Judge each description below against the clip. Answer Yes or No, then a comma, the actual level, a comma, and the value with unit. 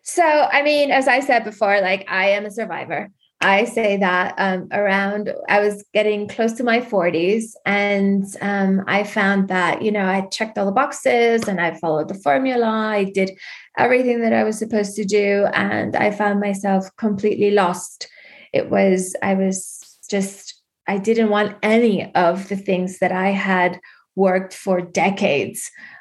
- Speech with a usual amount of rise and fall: No, narrow, 2.2 semitones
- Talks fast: No, average, 170 wpm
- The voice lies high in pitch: Yes, high, 200 Hz